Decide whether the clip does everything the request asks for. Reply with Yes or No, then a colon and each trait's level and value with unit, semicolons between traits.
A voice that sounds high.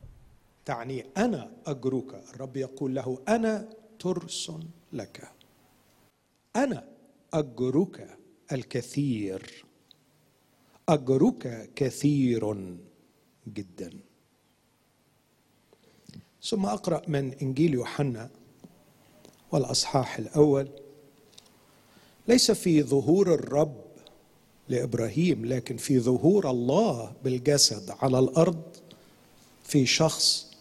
No: medium, 140 Hz